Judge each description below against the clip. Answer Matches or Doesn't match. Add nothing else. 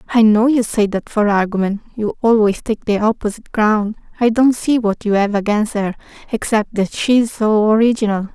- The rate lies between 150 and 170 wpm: Doesn't match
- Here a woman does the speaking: Matches